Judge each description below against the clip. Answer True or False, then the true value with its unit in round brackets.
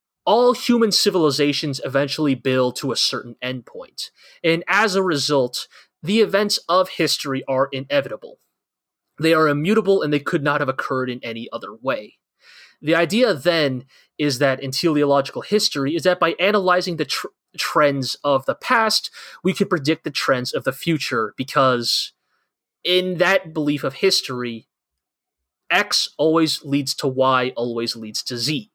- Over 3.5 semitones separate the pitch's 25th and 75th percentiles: True (5.4 semitones)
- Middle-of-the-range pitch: True (150 Hz)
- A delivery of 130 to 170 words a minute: True (150 wpm)